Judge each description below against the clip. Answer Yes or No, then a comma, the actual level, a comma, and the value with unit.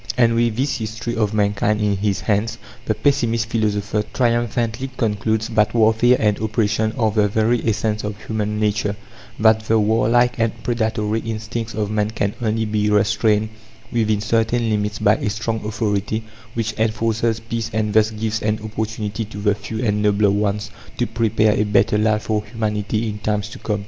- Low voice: Yes, low, 110 Hz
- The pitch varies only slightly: Yes, narrow, 1.3 semitones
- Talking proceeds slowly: No, average, 175 wpm